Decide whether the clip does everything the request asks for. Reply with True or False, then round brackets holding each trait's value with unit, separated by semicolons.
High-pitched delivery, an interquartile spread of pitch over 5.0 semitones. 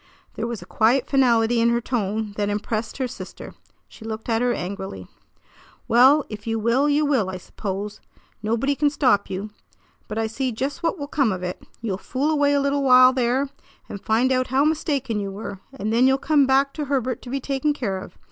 False (245 Hz; 4.2 semitones)